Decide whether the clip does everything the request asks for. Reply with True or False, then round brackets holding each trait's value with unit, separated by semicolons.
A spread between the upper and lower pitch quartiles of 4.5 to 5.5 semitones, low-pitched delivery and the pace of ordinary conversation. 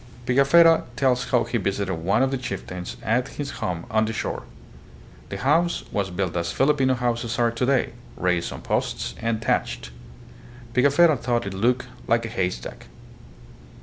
True (5.1 semitones; 120 Hz; 160 wpm)